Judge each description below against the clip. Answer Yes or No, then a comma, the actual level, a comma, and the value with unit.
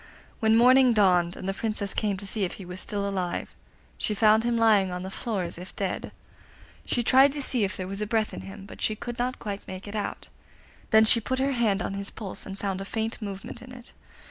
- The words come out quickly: Yes, fast, 235 wpm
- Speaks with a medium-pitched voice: No, high, 210 Hz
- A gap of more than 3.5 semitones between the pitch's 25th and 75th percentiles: No, average, 3.1 semitones